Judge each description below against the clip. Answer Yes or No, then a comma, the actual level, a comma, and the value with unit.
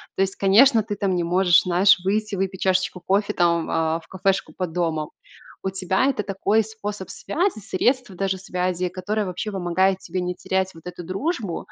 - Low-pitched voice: No, high, 190 Hz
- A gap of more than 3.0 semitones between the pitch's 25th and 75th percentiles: No, narrow, 2.4 semitones